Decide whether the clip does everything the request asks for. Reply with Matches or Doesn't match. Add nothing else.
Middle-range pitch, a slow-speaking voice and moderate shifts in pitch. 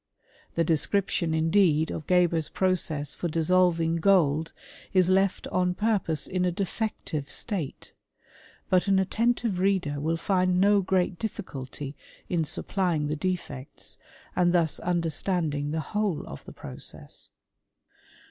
Matches